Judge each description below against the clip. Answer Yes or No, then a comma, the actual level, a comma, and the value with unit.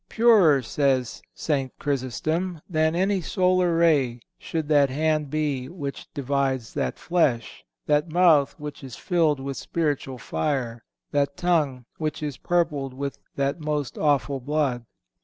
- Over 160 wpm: No, slow, 135 wpm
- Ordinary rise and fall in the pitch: Yes, average, 3.1 semitones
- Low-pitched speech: No, medium, 145 Hz